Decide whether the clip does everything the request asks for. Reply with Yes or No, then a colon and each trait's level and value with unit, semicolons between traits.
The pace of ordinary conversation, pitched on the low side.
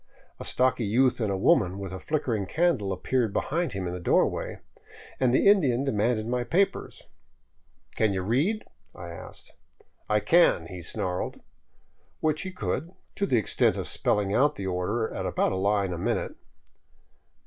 Yes: average, 175 wpm; low, 110 Hz